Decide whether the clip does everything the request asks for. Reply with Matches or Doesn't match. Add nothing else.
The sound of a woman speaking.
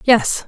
Matches